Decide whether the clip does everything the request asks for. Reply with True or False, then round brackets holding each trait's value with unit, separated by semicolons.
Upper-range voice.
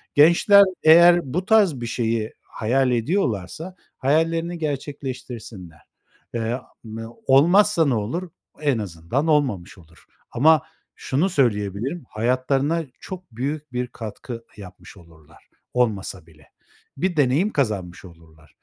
False (125 Hz)